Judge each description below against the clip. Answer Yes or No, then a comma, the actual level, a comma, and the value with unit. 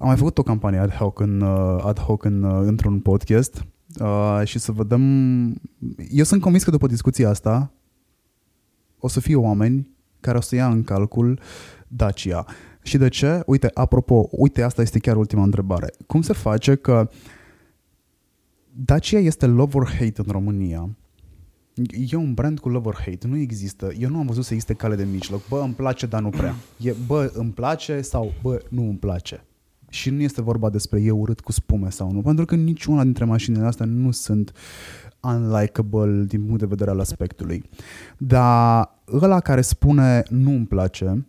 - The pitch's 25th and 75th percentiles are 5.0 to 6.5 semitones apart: No, average, 4.2 semitones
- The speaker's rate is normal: No, fast, 175 wpm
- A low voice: Yes, low, 115 Hz